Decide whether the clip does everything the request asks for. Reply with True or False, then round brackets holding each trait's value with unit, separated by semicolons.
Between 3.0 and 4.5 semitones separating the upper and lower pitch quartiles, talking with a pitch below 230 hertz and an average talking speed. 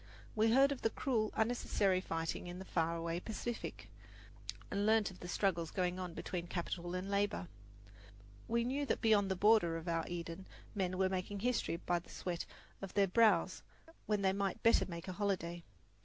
True (3.6 semitones; 190 Hz; 185 wpm)